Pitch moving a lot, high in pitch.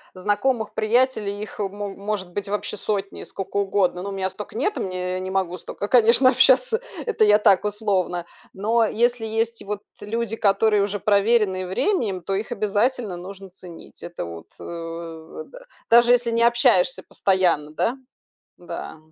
No: average, 3.6 semitones; high, 205 Hz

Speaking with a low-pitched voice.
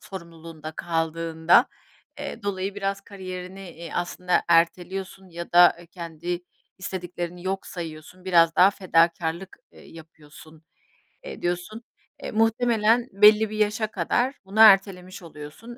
No: medium, 180 Hz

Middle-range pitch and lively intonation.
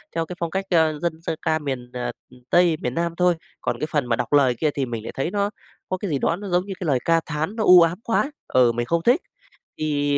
No: medium, 160 Hz; average, 4.3 semitones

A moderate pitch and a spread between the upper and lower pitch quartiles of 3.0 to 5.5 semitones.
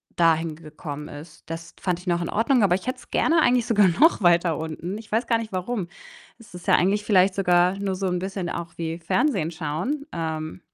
Yes: medium, 180 Hz; average, 4.0 semitones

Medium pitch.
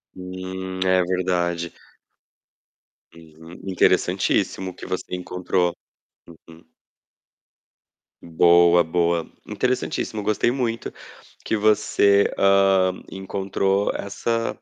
No: very low, 95 Hz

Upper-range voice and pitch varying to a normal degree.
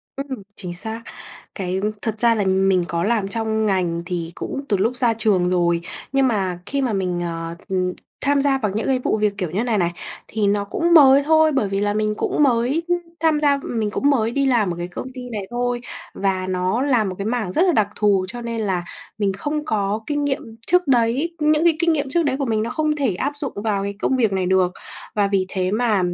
No: high, 220 Hz; wide, 5.8 semitones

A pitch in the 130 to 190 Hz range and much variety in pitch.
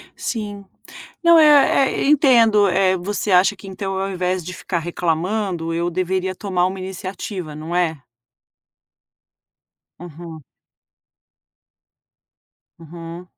No: medium, 185 Hz; average, 2.7 semitones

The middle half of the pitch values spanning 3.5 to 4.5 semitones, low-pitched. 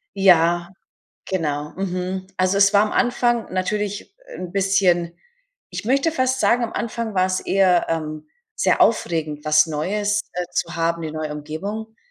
No: average, 4.1 semitones; medium, 185 Hz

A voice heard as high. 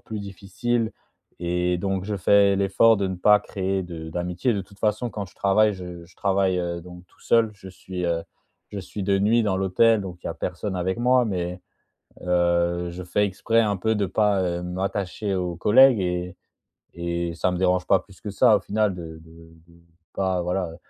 No: very low, 95 Hz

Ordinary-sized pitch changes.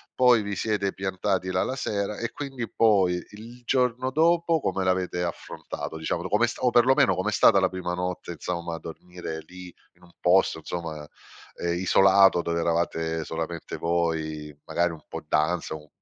Yes: average, 4.0 semitones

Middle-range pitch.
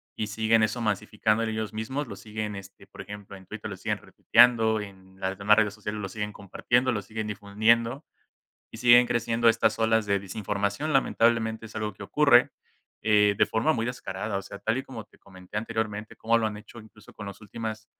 No: low, 110 Hz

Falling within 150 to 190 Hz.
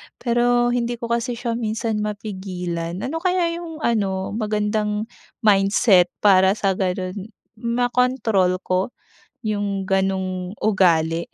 No: high, 210 Hz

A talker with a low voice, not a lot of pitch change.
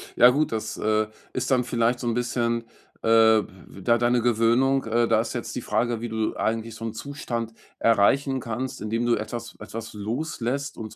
Yes: low, 115 Hz; narrow, 1.6 semitones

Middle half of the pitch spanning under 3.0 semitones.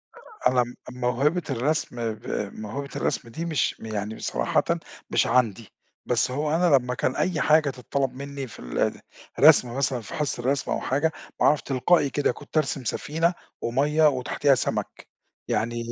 No: average, 3.7 semitones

